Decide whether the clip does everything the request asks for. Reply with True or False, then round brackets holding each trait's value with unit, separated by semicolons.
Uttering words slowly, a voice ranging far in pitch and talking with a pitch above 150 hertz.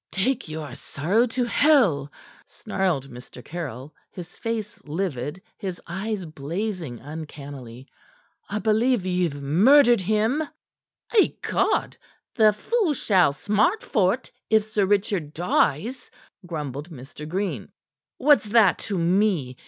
True (115 wpm; 6.6 semitones; 185 Hz)